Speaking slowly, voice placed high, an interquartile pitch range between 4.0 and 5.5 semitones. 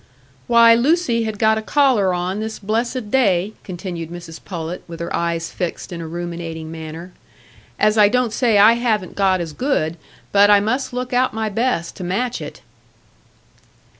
No: average, 170 wpm; high, 205 Hz; average, 5.1 semitones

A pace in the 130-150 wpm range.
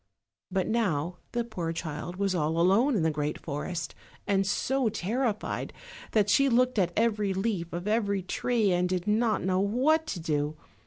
No: average, 170 wpm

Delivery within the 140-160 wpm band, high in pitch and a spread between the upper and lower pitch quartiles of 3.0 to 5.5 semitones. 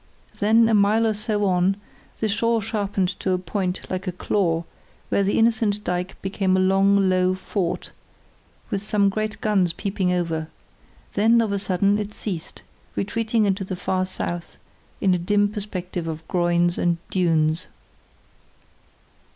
No: average, 150 wpm; high, 195 Hz; narrow, 2.6 semitones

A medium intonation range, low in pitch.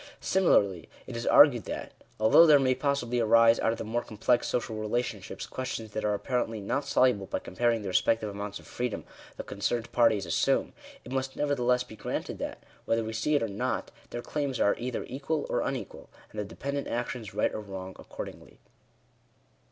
Yes: average, 3.3 semitones; low, 115 Hz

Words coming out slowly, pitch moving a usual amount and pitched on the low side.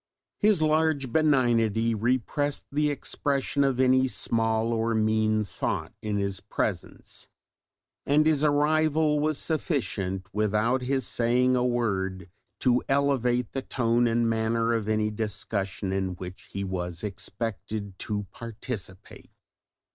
Yes: slow, 125 wpm; average, 4.4 semitones; low, 115 Hz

